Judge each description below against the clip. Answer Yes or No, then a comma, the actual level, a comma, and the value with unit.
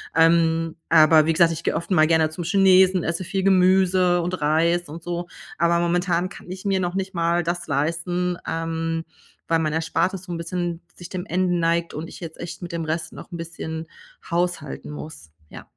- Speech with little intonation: Yes, narrow, 1.6 semitones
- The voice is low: No, medium, 170 Hz